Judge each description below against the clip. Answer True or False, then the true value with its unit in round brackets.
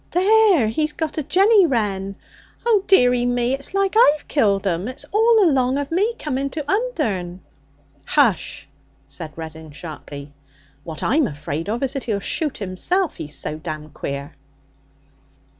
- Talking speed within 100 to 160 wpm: True (150 wpm)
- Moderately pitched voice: False (250 Hz)